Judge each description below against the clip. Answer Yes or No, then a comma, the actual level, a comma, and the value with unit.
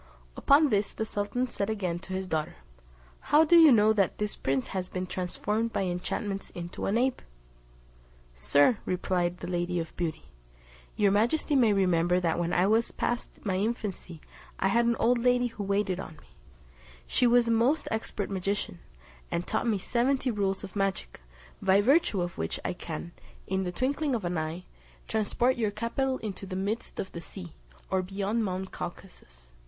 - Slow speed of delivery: No, average, 180 wpm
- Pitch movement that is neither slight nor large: Yes, average, 4.5 semitones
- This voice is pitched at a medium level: No, high, 200 Hz